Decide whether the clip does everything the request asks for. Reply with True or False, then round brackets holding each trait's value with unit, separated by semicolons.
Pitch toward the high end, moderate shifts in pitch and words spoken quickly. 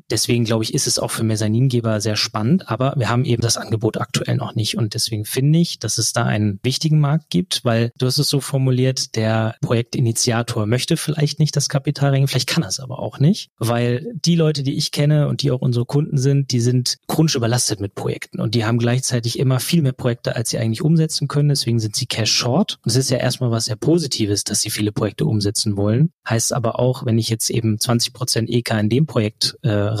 False (125 Hz; 3.8 semitones; 230 wpm)